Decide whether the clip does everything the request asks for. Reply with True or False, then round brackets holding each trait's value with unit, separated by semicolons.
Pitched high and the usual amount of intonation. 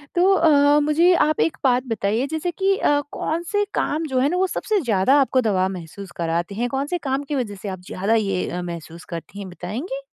False (255 Hz; 8.0 semitones)